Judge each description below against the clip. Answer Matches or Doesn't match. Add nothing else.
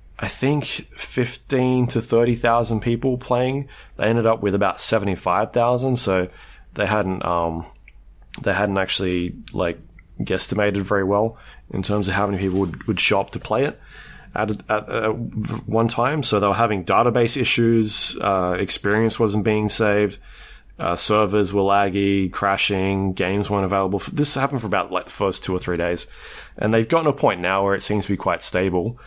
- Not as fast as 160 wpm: Doesn't match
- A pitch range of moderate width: Matches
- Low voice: Matches